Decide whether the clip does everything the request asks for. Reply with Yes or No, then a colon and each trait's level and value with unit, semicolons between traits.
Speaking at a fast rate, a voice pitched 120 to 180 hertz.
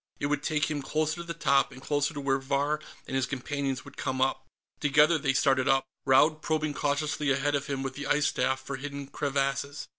Yes: fast, 215 wpm; medium, 140 Hz